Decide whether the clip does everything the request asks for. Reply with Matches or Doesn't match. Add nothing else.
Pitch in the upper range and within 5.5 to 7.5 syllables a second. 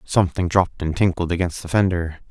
Doesn't match